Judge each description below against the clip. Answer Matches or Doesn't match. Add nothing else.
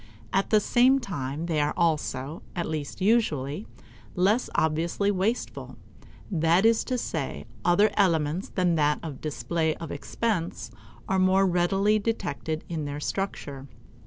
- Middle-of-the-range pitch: Matches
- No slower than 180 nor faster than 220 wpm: Doesn't match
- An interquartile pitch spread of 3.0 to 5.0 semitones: Matches